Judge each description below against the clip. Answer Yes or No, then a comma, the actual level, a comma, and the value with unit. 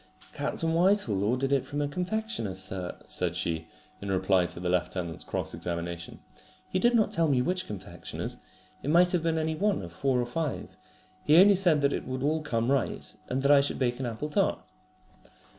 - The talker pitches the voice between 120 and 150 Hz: Yes, low, 135 Hz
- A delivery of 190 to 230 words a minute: Yes, average, 195 wpm